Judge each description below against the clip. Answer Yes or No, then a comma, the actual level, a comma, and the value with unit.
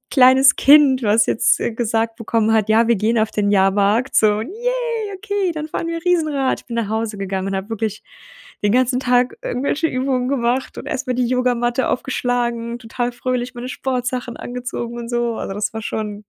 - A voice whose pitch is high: Yes, high, 245 Hz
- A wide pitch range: No, average, 2.8 semitones